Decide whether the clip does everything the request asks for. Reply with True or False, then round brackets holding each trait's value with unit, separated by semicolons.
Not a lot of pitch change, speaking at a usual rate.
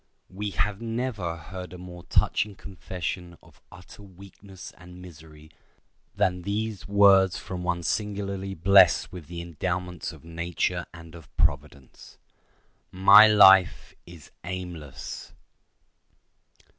False (2.3 semitones; 115 wpm)